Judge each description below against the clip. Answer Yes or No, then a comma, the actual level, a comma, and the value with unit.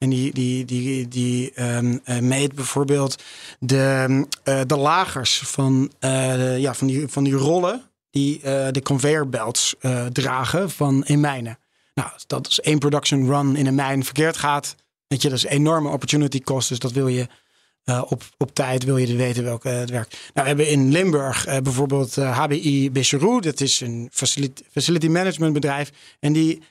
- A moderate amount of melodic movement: No, narrow, 2.0 semitones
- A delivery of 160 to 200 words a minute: Yes, average, 190 wpm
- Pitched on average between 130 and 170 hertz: Yes, low, 135 Hz